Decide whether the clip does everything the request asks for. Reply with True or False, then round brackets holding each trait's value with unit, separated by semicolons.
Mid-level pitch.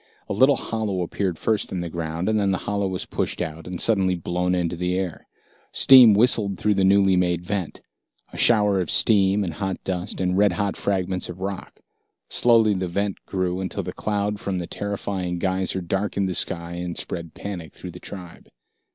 False (95 Hz)